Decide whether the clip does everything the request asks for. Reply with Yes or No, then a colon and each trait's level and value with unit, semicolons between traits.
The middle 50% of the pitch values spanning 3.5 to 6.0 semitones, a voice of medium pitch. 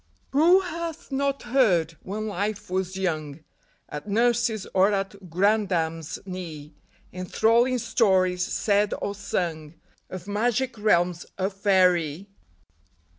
No: average, 4.1 semitones; high, 195 Hz